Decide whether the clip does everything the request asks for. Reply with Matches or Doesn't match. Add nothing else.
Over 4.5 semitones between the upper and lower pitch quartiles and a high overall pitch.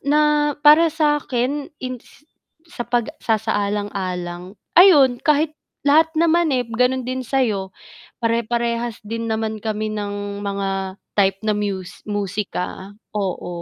Matches